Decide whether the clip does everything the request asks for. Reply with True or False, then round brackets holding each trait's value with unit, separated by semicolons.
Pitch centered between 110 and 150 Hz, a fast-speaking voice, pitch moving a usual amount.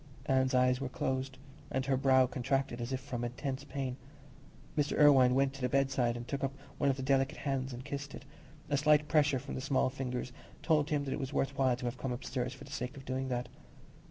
False (135 Hz; 230 wpm; 1.5 semitones)